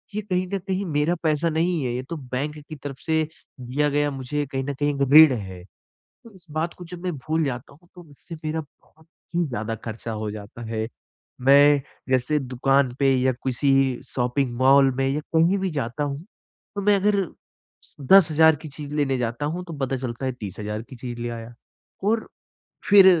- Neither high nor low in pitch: Yes, medium, 145 Hz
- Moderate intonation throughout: Yes, average, 4.2 semitones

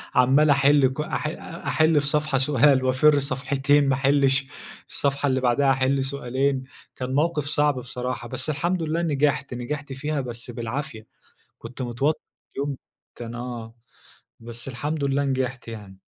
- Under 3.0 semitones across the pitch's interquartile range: Yes, narrow, 2.4 semitones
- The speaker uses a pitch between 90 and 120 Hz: No, low, 135 Hz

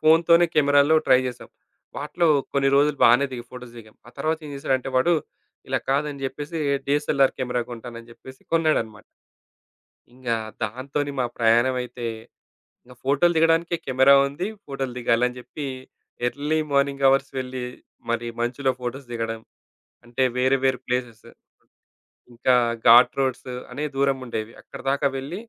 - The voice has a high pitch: No, low, 135 Hz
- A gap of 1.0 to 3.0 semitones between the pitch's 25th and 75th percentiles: Yes, average, 2.7 semitones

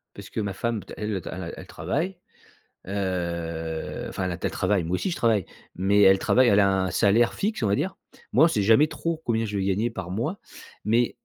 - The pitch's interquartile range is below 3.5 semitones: No, average, 3.9 semitones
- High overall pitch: No, low, 100 Hz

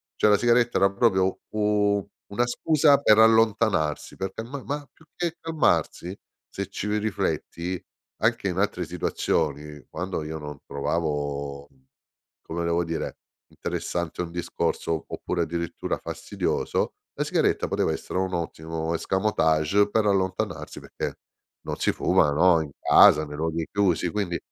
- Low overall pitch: Yes, very low, 90 Hz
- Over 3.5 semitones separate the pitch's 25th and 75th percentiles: Yes, average, 4.8 semitones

